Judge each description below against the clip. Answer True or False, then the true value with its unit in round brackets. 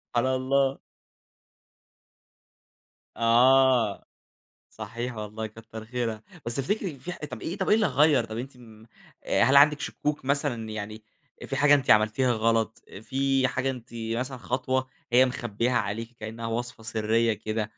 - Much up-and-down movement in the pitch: False (3.2 semitones)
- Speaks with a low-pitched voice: True (120 Hz)